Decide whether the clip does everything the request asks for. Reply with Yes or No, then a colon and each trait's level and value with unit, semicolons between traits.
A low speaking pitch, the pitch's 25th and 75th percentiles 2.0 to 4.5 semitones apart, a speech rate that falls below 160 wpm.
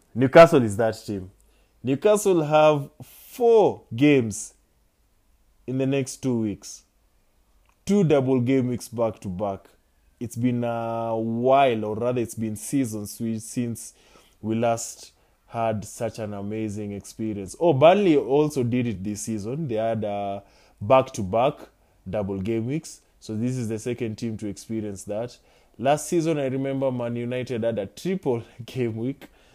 Yes: low, 115 Hz; average, 3.8 semitones; average, 150 wpm